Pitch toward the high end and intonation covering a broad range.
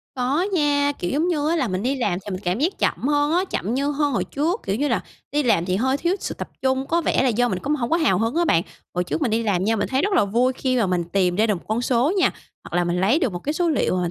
Yes: very high, 255 Hz; wide, 7.0 semitones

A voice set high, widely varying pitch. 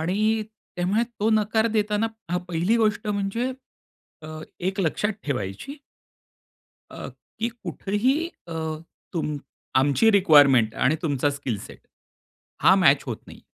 Yes: high, 195 Hz; wide, 6.7 semitones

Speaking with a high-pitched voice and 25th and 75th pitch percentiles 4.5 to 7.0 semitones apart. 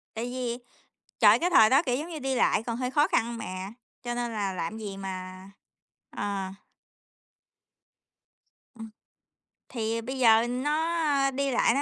No: high, 240 Hz; average, 3.8 semitones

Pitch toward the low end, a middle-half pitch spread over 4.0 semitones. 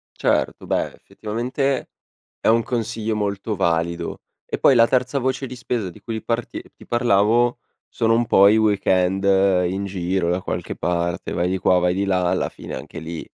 Yes: low, 105 Hz; average, 4.5 semitones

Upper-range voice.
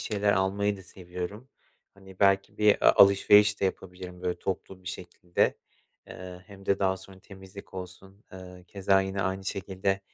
No: very low, 95 Hz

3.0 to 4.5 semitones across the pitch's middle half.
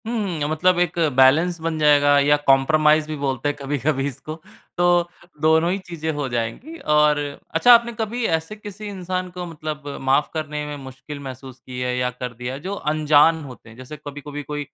Yes: average, 4.1 semitones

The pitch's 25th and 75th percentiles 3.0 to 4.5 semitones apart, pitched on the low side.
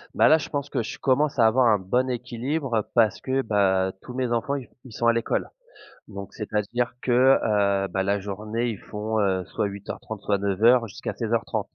Yes: average, 3.7 semitones; low, 110 Hz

